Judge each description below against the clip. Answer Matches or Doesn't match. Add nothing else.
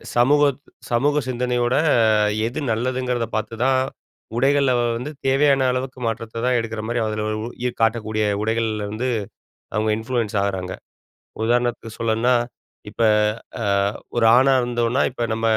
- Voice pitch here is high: Doesn't match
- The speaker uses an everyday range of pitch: Doesn't match